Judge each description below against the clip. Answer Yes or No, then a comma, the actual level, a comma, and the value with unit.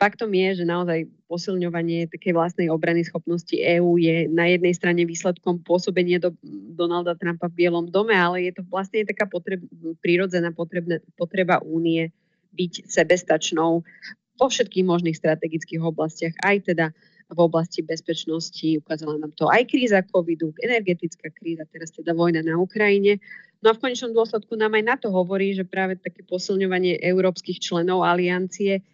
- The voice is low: No, medium, 175 Hz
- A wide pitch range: No, narrow, 2.4 semitones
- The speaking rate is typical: Yes, average, 150 wpm